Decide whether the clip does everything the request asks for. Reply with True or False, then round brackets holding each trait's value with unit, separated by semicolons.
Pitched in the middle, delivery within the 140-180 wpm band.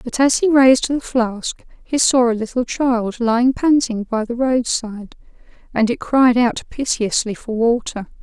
False (240 Hz; 170 wpm)